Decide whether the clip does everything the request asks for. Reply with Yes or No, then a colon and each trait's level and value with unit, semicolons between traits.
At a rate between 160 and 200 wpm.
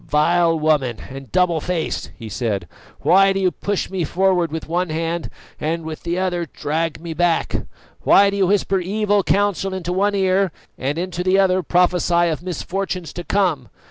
Yes: average, 175 wpm